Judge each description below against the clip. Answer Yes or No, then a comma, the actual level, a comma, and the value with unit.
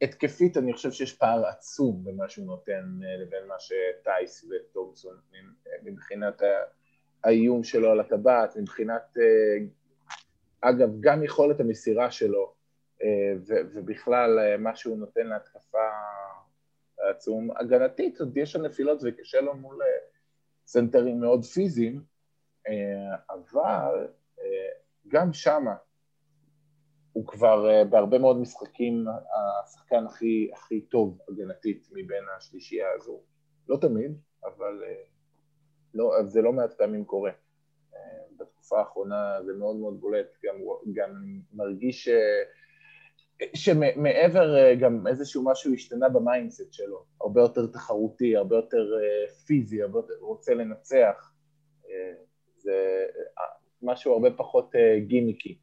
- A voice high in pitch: No, medium, 150 Hz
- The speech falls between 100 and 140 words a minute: Yes, average, 105 wpm